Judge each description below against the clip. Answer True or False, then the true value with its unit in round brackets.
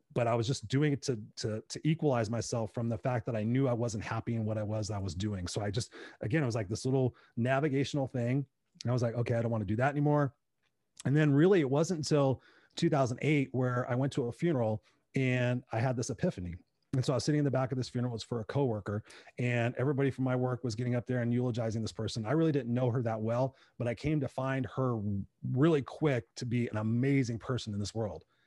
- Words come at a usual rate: False (255 wpm)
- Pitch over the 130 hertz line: False (125 Hz)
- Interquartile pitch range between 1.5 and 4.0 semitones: True (3.1 semitones)